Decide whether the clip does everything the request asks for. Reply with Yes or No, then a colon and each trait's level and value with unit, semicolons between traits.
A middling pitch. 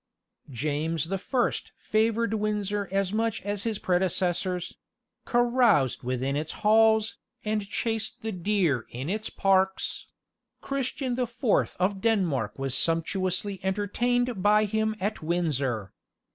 No: high, 200 Hz